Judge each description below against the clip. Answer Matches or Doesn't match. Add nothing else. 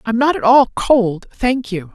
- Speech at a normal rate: Doesn't match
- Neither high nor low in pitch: Doesn't match